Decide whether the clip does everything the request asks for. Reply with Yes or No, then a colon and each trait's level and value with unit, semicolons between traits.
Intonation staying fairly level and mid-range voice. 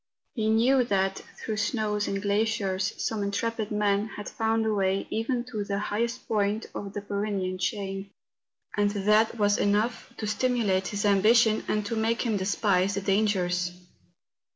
No: narrow, 1.9 semitones; high, 205 Hz